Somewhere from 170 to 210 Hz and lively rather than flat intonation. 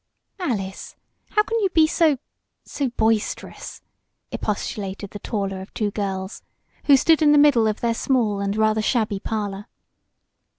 No: high, 220 Hz; wide, 5.7 semitones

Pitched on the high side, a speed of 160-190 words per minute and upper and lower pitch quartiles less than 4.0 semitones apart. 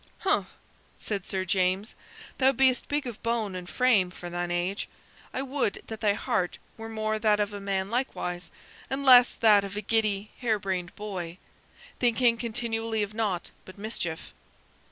Yes: high, 210 Hz; average, 165 wpm; average, 3.5 semitones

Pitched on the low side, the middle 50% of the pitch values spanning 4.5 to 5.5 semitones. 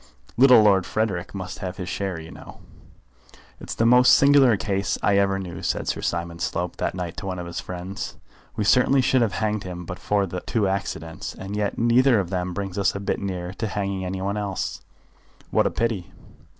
No: very low, 95 Hz; average, 2.9 semitones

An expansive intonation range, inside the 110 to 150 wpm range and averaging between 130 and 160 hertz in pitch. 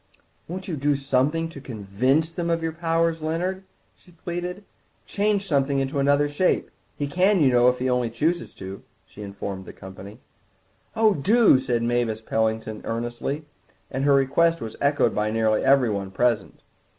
No: wide, 6.2 semitones; average, 160 wpm; medium, 140 Hz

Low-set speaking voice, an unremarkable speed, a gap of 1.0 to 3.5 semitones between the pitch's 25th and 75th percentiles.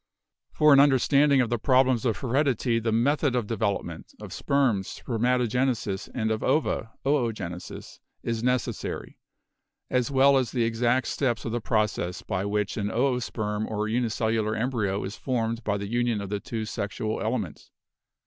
Yes: low, 115 Hz; average, 155 wpm; average, 2.9 semitones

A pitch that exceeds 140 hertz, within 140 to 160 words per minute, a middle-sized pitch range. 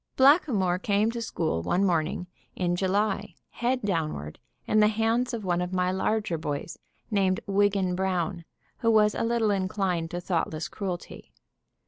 Yes: high, 190 Hz; average, 150 wpm; average, 3.4 semitones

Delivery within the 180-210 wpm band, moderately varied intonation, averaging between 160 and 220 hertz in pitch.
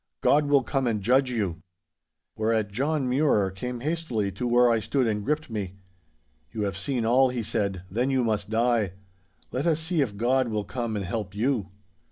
No: average, 190 wpm; average, 4.2 semitones; low, 120 Hz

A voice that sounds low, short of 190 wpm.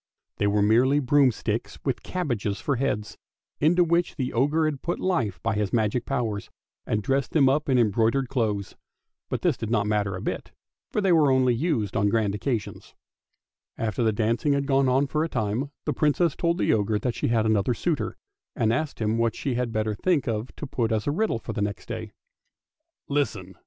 No: low, 120 Hz; average, 200 wpm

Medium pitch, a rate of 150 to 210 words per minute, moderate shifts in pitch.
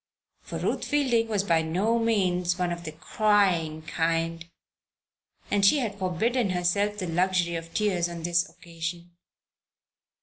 No: medium, 180 Hz; average, 140 wpm; average, 3.6 semitones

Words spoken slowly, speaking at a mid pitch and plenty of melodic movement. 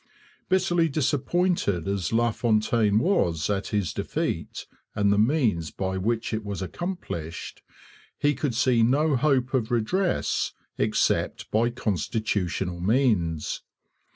No: slow, 115 wpm; low, 115 Hz; wide, 5.8 semitones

